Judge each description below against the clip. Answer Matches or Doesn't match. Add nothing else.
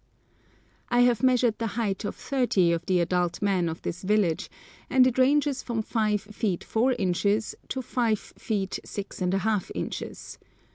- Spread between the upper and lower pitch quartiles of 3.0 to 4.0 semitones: Doesn't match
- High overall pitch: Matches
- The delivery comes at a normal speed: Matches